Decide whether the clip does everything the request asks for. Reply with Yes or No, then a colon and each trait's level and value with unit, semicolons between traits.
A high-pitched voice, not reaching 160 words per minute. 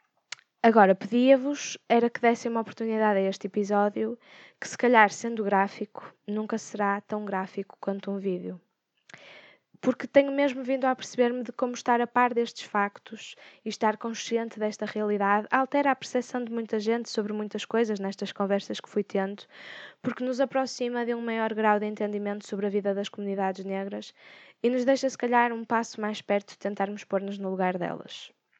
No: high, 215 Hz; average, 175 wpm